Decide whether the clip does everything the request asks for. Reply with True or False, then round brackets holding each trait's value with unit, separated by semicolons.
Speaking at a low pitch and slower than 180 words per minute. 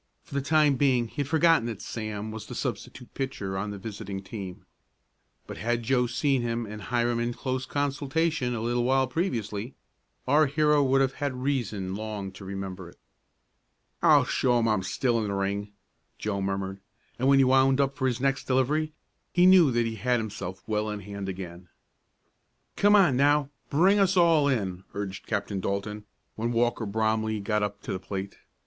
False (120 Hz; 185 wpm)